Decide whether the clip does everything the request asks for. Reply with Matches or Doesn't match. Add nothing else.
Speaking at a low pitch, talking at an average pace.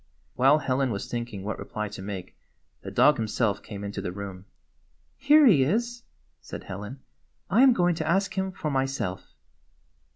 Matches